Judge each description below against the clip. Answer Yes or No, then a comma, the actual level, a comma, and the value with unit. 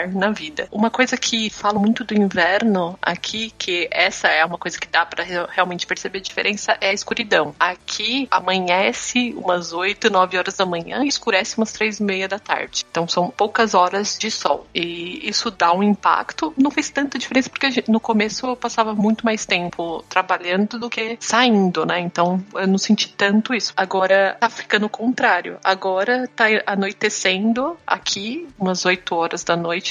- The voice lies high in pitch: Yes, high, 205 Hz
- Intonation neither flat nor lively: Yes, average, 3.8 semitones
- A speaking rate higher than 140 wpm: Yes, fast, 185 wpm